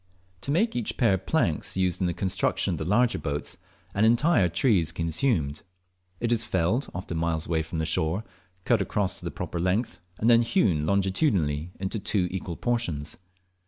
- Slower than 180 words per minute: No, average, 185 wpm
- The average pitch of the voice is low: Yes, very low, 95 Hz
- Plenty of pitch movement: Yes, wide, 5.8 semitones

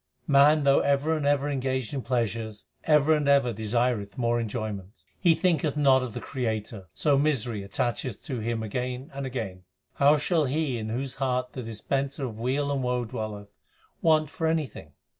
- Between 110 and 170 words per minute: No, average, 180 wpm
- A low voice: Yes, low, 130 Hz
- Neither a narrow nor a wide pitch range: Yes, average, 4.0 semitones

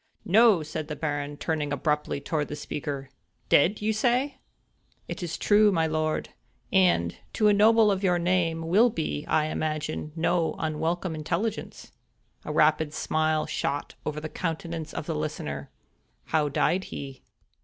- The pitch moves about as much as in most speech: Yes, average, 3.2 semitones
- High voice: No, medium, 160 Hz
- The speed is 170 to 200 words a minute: No, average, 155 wpm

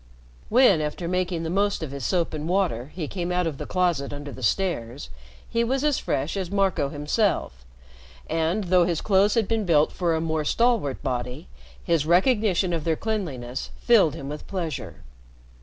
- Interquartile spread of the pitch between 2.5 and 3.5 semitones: No, average, 5.0 semitones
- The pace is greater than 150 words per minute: Yes, average, 180 wpm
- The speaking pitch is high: No, medium, 170 Hz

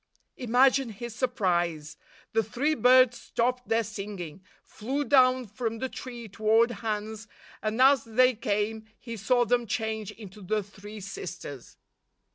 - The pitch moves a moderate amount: Yes, average, 3.1 semitones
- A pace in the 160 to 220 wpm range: No, slow, 135 wpm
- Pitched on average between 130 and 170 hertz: No, high, 225 Hz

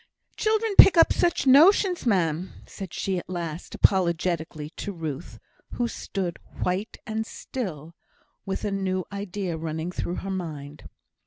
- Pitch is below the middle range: No, medium, 185 Hz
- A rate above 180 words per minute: No, average, 140 wpm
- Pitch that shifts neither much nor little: Yes, average, 4.6 semitones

